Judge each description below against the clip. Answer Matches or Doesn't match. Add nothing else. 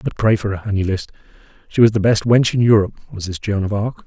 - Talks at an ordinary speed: Doesn't match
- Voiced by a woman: Doesn't match